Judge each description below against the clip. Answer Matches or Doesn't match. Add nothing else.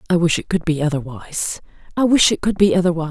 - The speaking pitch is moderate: Matches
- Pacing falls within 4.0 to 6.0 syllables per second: Doesn't match